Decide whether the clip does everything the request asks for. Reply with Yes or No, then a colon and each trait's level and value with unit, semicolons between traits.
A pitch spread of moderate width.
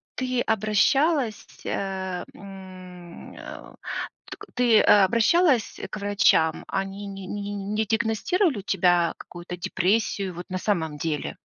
Yes: average, 3.3 semitones